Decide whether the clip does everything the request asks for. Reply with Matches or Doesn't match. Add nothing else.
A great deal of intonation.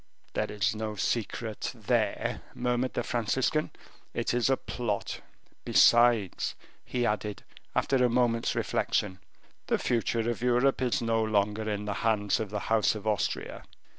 Doesn't match